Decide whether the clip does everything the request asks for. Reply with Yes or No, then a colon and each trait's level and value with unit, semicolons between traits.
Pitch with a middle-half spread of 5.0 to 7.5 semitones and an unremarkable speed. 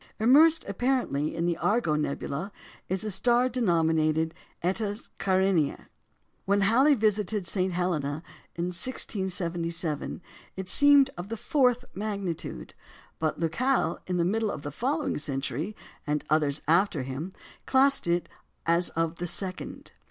No: average, 5.3 semitones; slow, 130 wpm